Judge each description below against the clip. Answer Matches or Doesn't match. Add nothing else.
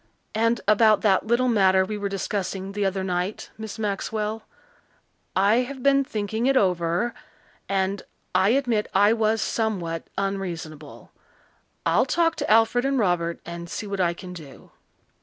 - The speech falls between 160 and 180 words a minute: Doesn't match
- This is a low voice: Doesn't match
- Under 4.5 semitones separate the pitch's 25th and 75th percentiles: Matches